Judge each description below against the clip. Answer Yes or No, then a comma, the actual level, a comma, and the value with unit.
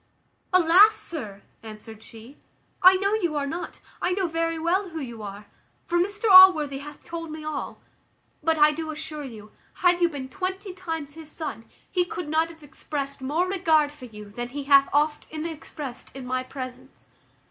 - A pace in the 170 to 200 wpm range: Yes, average, 180 wpm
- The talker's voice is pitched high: Yes, very high, 310 Hz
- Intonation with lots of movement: No, average, 4.2 semitones